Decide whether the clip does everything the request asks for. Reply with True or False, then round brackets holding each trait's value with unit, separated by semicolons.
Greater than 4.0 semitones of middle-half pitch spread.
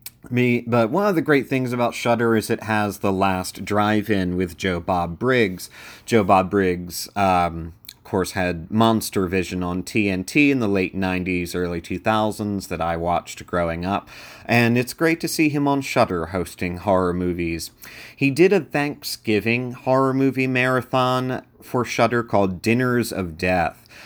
True (5.2 semitones)